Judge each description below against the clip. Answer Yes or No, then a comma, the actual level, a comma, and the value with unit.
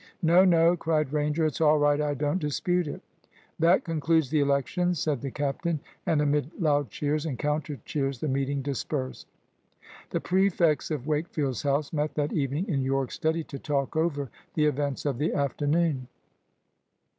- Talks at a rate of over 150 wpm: Yes, average, 165 wpm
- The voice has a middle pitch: Yes, medium, 150 Hz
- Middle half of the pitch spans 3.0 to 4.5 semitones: No, narrow, 2.4 semitones